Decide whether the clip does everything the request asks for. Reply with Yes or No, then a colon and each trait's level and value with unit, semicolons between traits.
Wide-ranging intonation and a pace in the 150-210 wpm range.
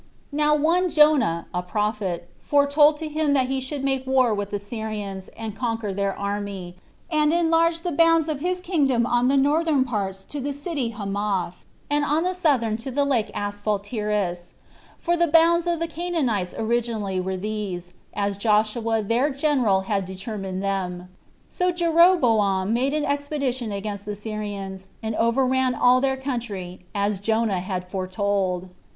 Yes: wide, 6.3 semitones; average, 155 wpm